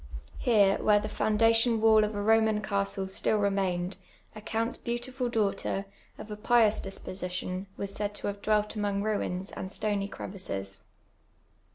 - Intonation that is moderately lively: No, narrow, 1.9 semitones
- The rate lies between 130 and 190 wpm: Yes, average, 155 wpm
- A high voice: Yes, high, 205 Hz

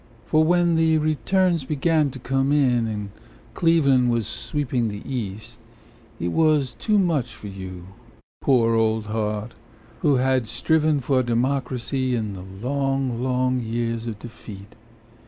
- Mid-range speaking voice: No, low, 125 Hz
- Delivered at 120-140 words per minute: Yes, slow, 135 wpm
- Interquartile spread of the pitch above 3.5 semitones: Yes, average, 4.5 semitones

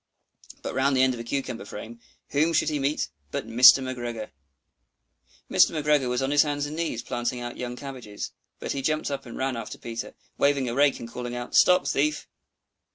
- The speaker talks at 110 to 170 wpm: No, average, 200 wpm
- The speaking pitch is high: No, low, 130 Hz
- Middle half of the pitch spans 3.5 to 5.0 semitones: No, average, 3.0 semitones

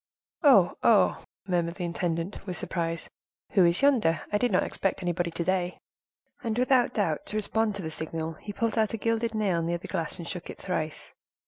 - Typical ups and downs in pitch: Yes, average, 4.4 semitones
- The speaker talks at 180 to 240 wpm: Yes, average, 200 wpm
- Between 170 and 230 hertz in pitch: Yes, medium, 185 Hz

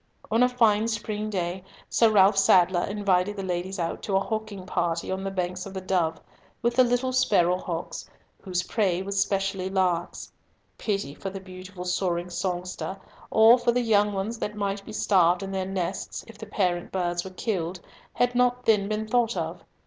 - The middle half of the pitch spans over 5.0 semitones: No, average, 2.9 semitones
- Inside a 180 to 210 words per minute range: Yes, average, 185 wpm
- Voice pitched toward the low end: No, high, 195 Hz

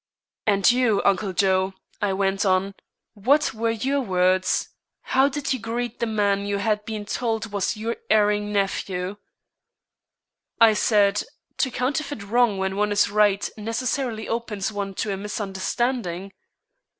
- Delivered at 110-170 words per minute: Yes, average, 140 wpm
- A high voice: Yes, high, 210 Hz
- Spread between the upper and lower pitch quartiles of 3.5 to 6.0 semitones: No, average, 2.7 semitones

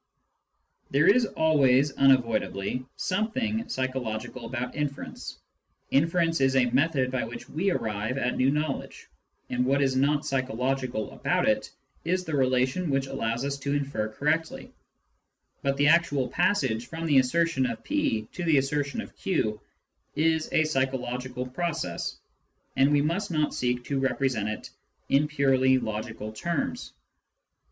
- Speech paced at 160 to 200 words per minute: No, average, 145 wpm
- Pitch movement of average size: Yes, average, 3.7 semitones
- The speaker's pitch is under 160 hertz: Yes, low, 135 Hz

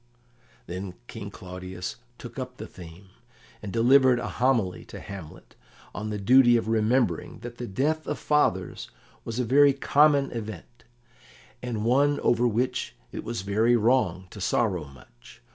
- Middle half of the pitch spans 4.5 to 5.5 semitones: Yes, average, 4.8 semitones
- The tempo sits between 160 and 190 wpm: No, average, 150 wpm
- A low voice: Yes, low, 115 Hz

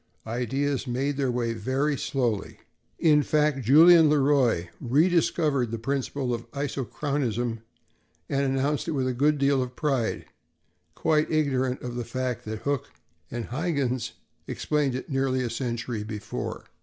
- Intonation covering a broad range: No, average, 3.1 semitones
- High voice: No, low, 135 Hz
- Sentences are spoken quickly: No, average, 145 wpm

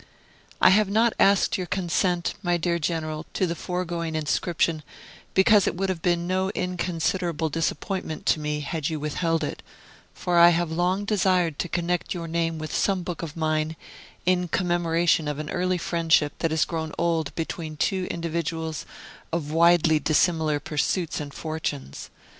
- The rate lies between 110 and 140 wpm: No, average, 160 wpm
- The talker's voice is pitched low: No, medium, 170 Hz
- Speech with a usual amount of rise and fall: No, narrow, 2.2 semitones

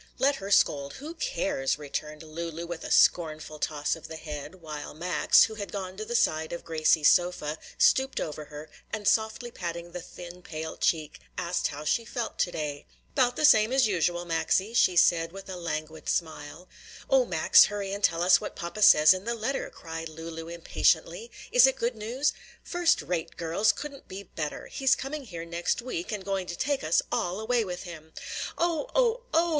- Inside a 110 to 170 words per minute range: No, average, 195 wpm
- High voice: No, medium, 180 Hz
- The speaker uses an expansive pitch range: Yes, wide, 6.2 semitones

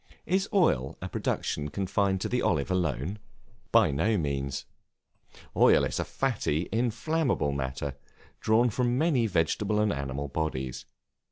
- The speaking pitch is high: No, very low, 95 Hz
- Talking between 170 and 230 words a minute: No, slow, 135 wpm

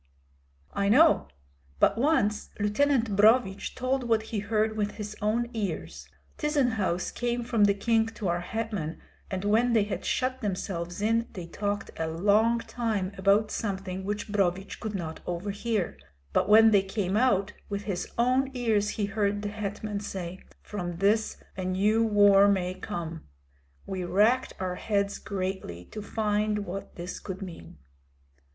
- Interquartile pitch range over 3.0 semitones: No, average, 2.7 semitones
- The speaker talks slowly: No, average, 155 wpm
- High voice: Yes, high, 205 Hz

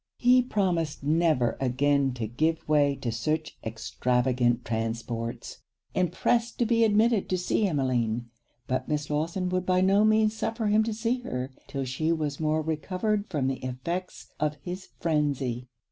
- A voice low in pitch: No, medium, 155 Hz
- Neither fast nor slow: Yes, average, 160 wpm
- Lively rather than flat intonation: Yes, wide, 6.7 semitones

